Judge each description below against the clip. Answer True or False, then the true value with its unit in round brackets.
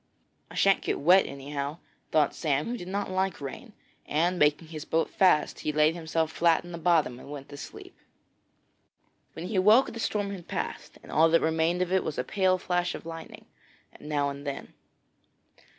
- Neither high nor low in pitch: True (165 Hz)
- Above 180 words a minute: True (190 wpm)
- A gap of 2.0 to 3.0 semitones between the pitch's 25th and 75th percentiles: False (3.7 semitones)